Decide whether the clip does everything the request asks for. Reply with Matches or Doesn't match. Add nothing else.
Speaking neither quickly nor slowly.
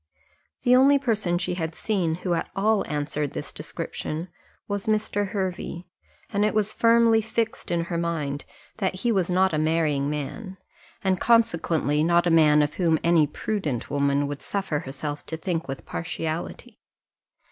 Matches